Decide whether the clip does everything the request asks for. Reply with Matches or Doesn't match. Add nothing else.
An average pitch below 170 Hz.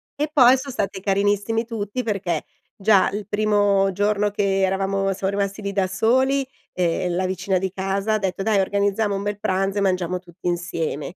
Doesn't match